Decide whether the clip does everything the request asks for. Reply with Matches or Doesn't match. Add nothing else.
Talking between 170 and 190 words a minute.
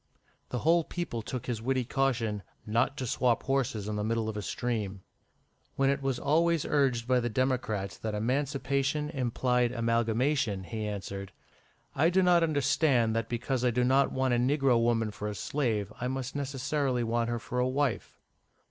Matches